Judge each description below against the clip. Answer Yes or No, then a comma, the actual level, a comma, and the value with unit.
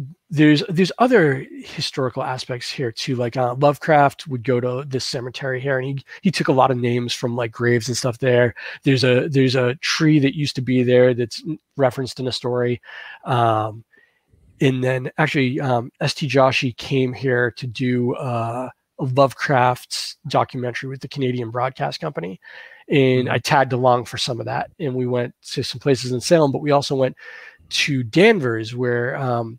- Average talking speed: Yes, average, 180 wpm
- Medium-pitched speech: No, low, 130 Hz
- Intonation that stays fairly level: Yes, narrow, 2.3 semitones